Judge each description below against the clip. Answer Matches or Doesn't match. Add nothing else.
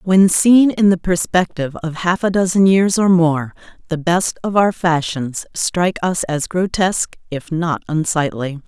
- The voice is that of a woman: Matches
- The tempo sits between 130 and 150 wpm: Doesn't match